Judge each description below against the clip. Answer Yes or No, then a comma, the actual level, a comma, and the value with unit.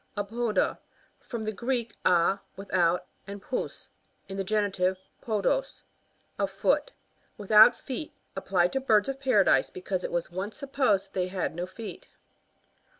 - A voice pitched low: No, high, 205 Hz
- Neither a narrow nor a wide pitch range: Yes, average, 4.0 semitones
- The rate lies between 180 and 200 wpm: No, average, 145 wpm